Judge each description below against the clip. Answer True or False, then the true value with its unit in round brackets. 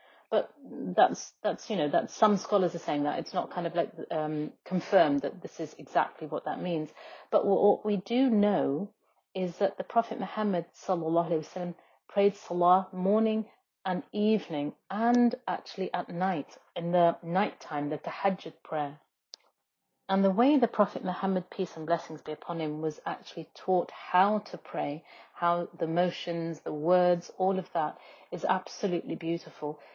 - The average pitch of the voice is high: False (180 Hz)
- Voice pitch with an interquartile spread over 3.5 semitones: False (3.2 semitones)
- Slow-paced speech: False (160 wpm)